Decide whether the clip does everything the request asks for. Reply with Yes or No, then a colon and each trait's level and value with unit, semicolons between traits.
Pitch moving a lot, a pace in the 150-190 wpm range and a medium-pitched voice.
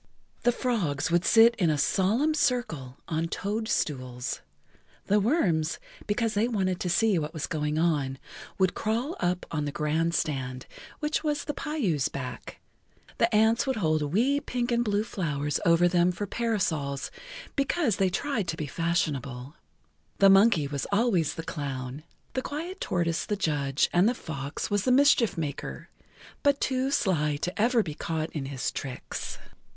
Yes: wide, 7.5 semitones; average, 165 wpm; medium, 180 Hz